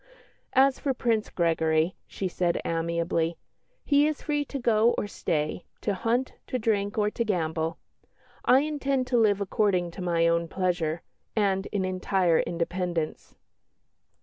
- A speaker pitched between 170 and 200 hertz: Yes, high, 190 Hz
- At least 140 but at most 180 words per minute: Yes, average, 145 wpm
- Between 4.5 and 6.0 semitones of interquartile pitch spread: Yes, wide, 5.5 semitones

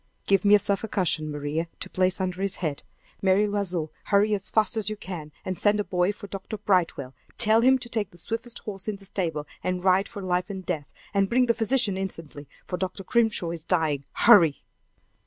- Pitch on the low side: No, high, 190 Hz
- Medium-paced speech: No, fast, 210 wpm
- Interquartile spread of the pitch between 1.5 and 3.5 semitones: Yes, average, 3.1 semitones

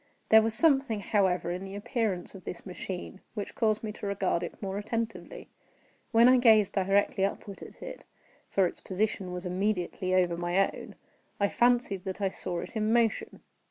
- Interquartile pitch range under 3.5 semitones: Yes, average, 3.1 semitones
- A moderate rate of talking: Yes, average, 180 wpm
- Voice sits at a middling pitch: No, high, 200 Hz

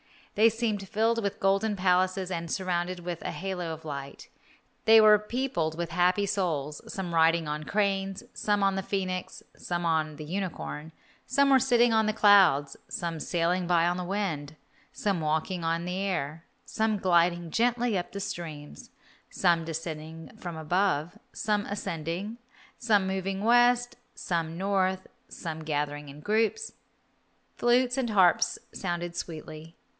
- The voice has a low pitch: No, medium, 185 Hz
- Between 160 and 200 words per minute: No, average, 150 wpm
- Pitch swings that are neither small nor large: Yes, average, 3.9 semitones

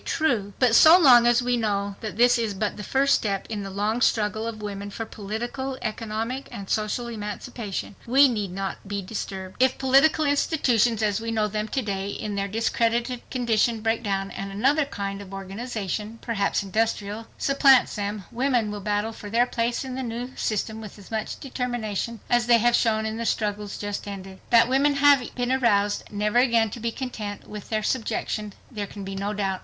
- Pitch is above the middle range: Yes, high, 220 Hz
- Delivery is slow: No, average, 190 wpm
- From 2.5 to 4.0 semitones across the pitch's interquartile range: Yes, average, 3.0 semitones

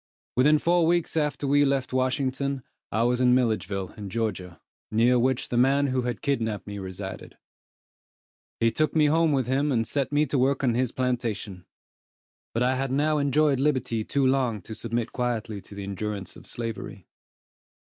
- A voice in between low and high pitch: No, low, 125 Hz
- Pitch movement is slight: No, average, 3.8 semitones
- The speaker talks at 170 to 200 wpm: Yes, average, 175 wpm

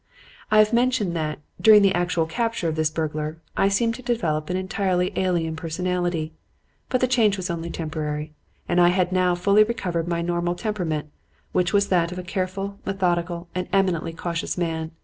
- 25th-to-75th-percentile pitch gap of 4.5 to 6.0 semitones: No, average, 3.0 semitones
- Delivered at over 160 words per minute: Yes, average, 180 wpm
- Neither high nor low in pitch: Yes, medium, 180 Hz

